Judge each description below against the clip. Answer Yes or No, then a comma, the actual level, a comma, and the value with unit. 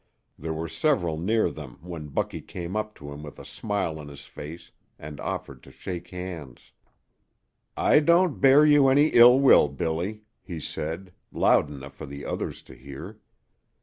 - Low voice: Yes, very low, 85 Hz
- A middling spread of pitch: No, wide, 6.6 semitones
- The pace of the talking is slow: No, average, 170 wpm